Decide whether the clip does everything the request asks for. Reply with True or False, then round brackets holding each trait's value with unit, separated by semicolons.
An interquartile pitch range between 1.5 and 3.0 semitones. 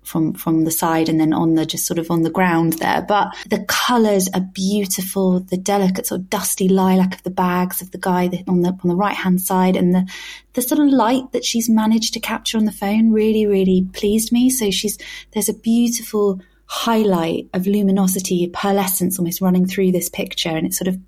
True (2.6 semitones)